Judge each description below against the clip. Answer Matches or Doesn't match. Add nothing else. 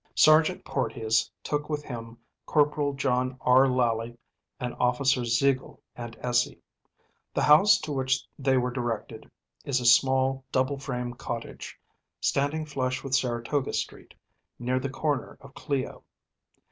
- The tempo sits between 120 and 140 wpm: Matches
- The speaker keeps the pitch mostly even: Matches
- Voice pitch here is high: Doesn't match